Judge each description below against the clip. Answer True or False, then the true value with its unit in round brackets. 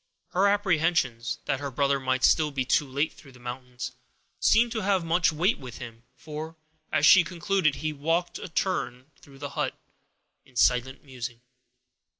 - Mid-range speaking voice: True (145 Hz)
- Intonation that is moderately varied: True (4.9 semitones)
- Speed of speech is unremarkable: True (175 wpm)